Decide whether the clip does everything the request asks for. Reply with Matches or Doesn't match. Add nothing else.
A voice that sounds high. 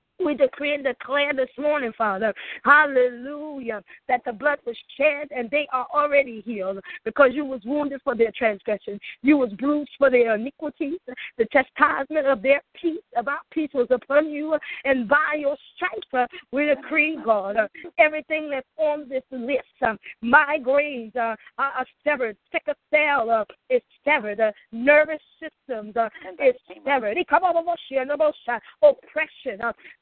Matches